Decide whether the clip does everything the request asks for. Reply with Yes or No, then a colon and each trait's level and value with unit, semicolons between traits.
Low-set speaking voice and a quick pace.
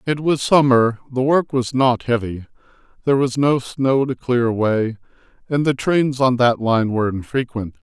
No: low, 125 Hz; average, 175 wpm